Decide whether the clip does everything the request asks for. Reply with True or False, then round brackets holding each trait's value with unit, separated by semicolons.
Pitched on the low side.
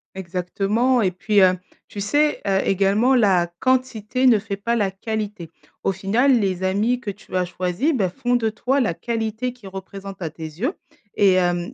False (200 Hz)